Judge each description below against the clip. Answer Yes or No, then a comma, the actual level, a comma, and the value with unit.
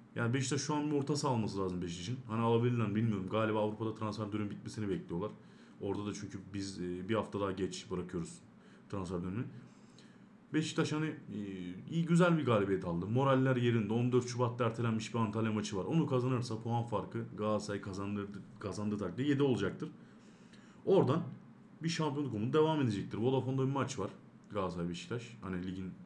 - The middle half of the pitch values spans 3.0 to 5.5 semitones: Yes, average, 4.6 semitones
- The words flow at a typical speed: No, fast, 160 wpm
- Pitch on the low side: Yes, low, 110 Hz